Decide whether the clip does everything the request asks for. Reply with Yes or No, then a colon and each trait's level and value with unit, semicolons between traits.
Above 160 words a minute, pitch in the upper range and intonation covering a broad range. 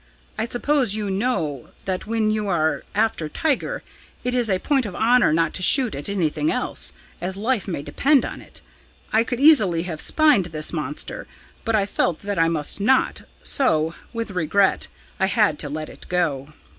Yes: average, 180 wpm; high, 200 Hz; wide, 6.6 semitones